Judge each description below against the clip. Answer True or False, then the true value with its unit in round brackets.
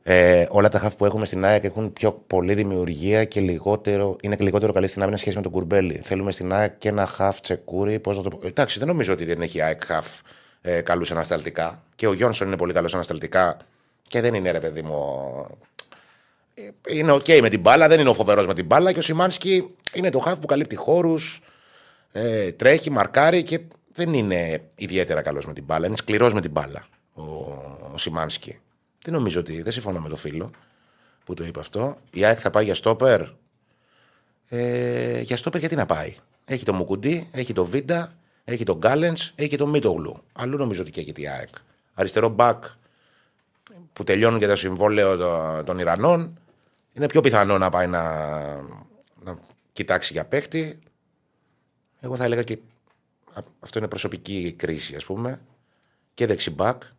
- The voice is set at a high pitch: False (105 Hz)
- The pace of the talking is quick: True (185 wpm)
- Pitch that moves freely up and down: True (6.7 semitones)